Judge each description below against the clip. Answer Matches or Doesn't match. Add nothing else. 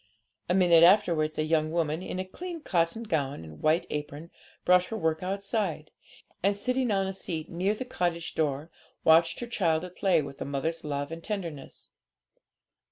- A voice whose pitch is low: Doesn't match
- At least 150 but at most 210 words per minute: Matches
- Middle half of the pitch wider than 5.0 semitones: Doesn't match